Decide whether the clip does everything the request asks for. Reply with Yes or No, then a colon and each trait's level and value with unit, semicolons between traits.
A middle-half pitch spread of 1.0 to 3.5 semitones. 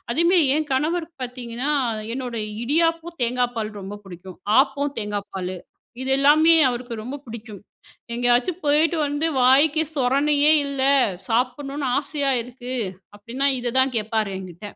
No: average, 4.0 semitones